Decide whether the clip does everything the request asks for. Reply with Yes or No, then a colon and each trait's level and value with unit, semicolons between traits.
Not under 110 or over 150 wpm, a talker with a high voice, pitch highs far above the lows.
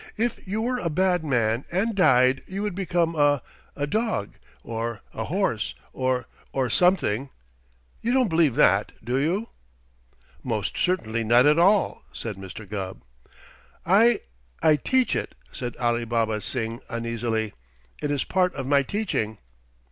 No: average, 145 wpm; low, 135 Hz; wide, 8.1 semitones